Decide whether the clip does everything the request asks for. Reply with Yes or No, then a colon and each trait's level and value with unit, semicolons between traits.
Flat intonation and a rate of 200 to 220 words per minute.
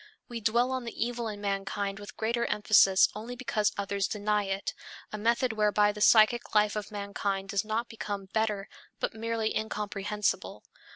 No: narrow, 1.9 semitones; average, 165 wpm